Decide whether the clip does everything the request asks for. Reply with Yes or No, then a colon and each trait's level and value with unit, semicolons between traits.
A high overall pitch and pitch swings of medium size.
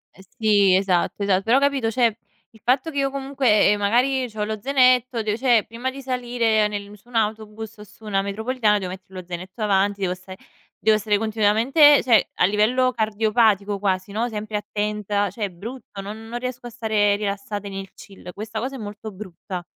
Yes: high, 215 Hz; average, 3.0 semitones